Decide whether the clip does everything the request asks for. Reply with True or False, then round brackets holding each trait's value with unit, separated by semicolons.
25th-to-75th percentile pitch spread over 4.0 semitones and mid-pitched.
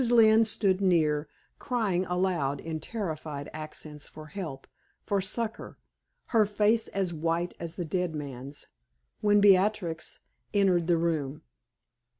True (4.7 semitones; 175 Hz)